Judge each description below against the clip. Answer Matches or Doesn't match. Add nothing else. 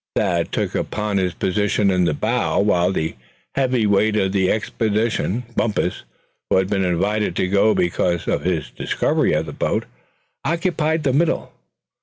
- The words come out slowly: Doesn't match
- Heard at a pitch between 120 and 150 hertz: Doesn't match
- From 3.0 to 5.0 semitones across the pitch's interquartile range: Matches